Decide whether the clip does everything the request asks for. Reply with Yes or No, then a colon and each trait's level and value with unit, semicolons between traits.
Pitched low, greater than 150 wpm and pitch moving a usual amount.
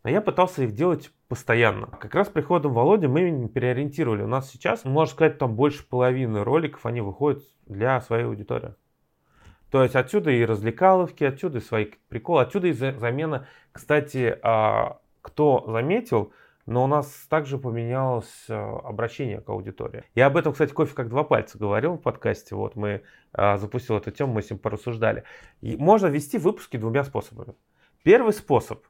Yes: low, 130 Hz; fast, 160 wpm; average, 4.6 semitones